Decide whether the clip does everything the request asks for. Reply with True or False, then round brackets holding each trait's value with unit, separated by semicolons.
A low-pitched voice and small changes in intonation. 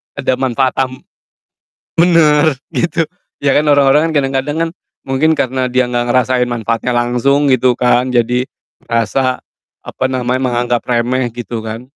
True (130 Hz; 1.9 semitones)